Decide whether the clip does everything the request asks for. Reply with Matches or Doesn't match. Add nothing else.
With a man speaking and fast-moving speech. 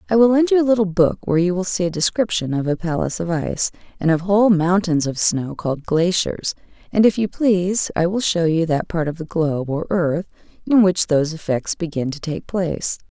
Doesn't match